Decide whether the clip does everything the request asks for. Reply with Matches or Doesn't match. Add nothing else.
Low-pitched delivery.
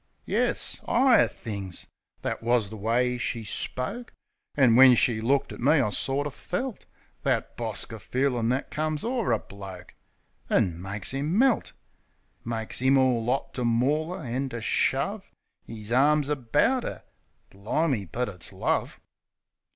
Matches